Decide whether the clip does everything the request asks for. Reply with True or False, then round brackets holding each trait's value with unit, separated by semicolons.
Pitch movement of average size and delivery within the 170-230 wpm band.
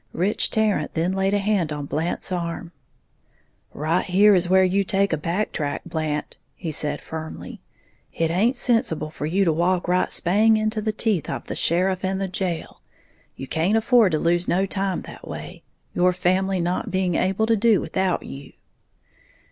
True (3.0 semitones; 180 wpm)